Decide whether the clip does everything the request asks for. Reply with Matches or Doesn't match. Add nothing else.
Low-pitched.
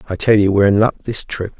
Matches